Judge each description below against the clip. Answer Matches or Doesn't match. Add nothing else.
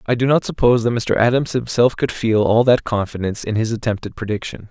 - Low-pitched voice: Matches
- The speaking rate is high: Matches